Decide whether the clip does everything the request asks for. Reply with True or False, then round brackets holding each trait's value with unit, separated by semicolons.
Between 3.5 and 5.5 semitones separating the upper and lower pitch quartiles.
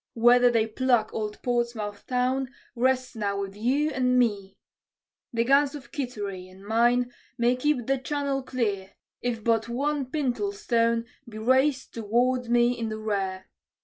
False (3.0 semitones)